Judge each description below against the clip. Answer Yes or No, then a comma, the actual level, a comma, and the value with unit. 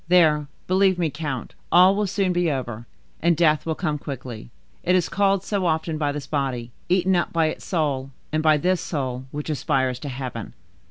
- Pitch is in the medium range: Yes, medium, 155 Hz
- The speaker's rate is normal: Yes, average, 195 wpm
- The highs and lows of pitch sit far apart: No, average, 4.7 semitones